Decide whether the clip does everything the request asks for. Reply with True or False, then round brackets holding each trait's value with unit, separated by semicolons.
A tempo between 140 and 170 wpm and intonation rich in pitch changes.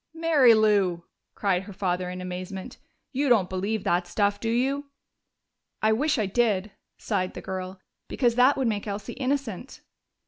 False (160 wpm; 4.9 semitones)